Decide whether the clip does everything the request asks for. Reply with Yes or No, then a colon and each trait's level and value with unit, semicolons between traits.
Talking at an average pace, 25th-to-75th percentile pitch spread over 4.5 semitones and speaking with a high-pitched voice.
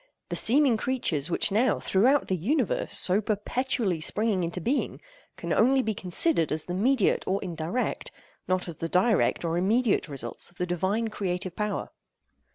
Yes: average, 165 wpm; average, 5.3 semitones; high, 195 Hz